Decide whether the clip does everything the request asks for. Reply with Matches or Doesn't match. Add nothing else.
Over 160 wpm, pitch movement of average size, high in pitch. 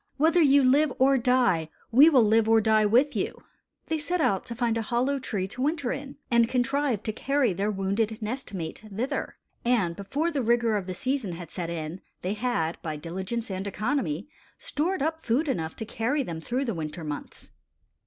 Doesn't match